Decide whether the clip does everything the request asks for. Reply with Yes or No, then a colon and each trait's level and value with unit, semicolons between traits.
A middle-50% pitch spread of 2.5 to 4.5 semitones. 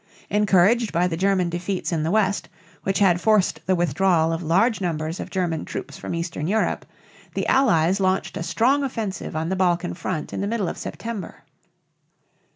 Yes: average, 3.3 semitones